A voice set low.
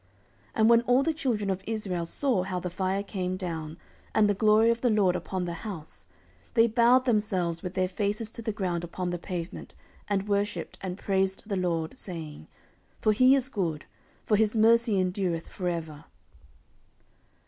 No: high, 195 Hz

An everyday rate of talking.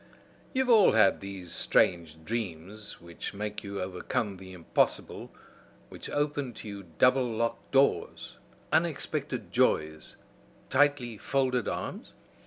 No: slow, 120 wpm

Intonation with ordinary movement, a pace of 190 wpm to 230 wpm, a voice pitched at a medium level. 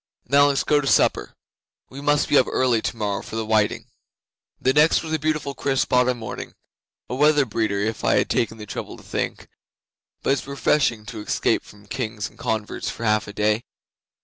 No: average, 4.7 semitones; average, 195 wpm; low, 120 Hz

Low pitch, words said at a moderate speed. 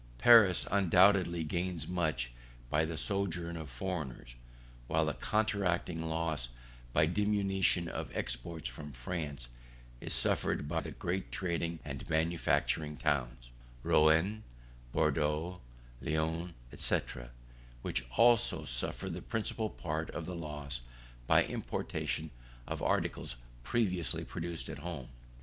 No: very low, 85 Hz; slow, 115 wpm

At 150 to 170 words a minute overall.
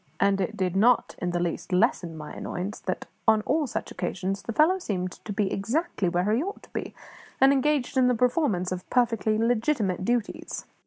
No: average, 195 wpm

